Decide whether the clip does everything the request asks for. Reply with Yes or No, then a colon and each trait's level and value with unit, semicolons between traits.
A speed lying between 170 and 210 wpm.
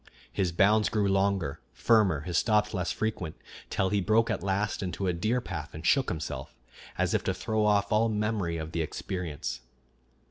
Yes: average, 180 wpm